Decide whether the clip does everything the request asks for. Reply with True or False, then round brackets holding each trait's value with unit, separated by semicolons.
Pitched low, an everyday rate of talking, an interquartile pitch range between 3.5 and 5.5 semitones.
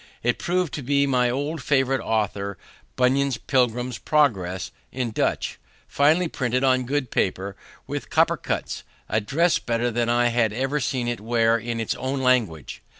False (125 Hz; 160 wpm; 3.0 semitones)